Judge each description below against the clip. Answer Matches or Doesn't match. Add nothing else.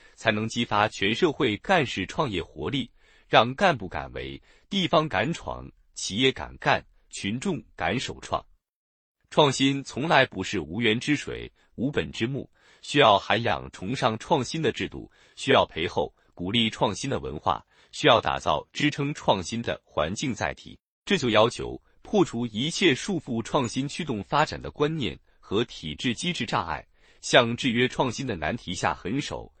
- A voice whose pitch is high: Doesn't match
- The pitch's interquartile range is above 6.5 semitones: Doesn't match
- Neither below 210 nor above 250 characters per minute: Matches